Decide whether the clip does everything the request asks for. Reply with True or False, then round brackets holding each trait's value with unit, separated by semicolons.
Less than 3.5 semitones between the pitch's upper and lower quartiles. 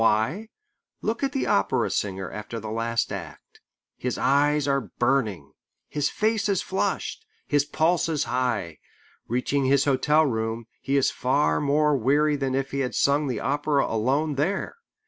False (4.4 semitones)